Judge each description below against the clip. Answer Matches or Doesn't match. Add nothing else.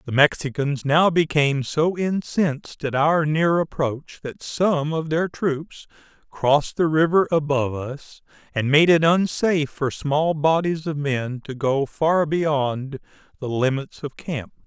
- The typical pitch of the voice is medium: Matches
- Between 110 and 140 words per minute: Doesn't match